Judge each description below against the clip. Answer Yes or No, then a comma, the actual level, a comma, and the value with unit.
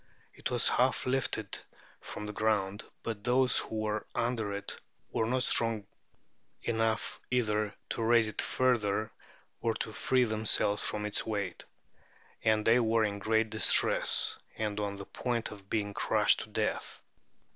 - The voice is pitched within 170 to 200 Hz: No, low, 110 Hz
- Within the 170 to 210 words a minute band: No, average, 150 wpm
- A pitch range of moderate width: No, narrow, 1.9 semitones